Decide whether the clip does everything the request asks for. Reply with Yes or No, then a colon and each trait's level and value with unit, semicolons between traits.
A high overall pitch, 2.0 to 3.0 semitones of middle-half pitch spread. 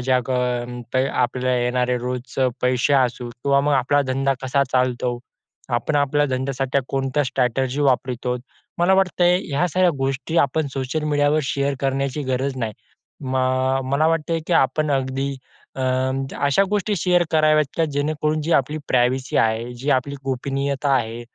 No: low, 135 Hz; narrow, 2.5 semitones